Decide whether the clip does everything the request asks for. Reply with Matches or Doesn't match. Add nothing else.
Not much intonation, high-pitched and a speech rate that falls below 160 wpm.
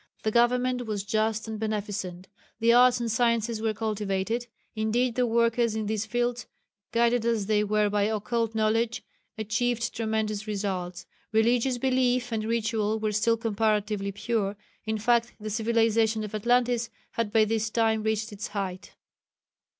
Matches